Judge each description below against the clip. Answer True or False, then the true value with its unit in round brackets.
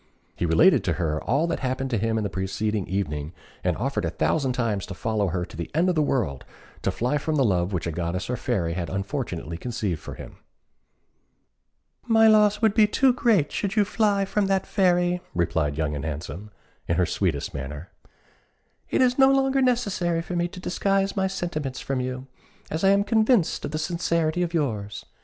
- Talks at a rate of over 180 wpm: True (200 wpm)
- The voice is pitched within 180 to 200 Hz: False (135 Hz)